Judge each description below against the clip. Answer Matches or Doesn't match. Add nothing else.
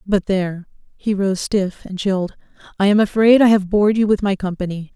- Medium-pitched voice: Doesn't match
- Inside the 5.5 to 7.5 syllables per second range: Matches